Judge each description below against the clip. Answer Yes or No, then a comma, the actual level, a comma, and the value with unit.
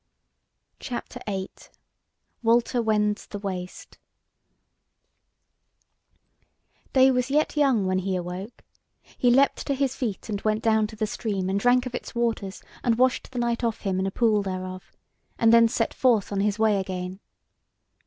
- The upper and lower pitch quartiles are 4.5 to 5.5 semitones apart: No, average, 3.9 semitones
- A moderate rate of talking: Yes, average, 155 wpm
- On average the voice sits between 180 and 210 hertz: No, high, 220 Hz